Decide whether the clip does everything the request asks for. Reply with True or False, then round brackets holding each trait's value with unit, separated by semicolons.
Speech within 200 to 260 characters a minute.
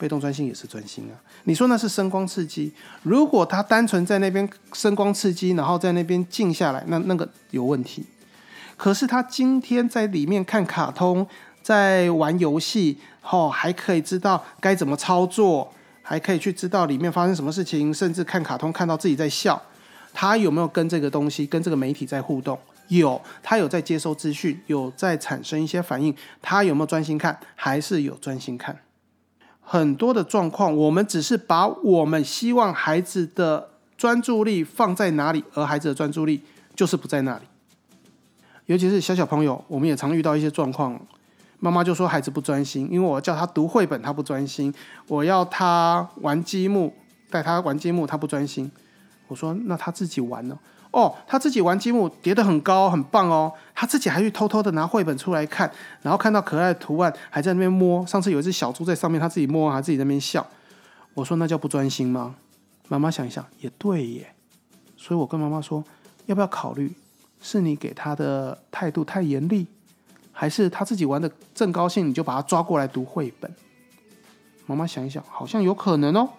False (290 characters per minute)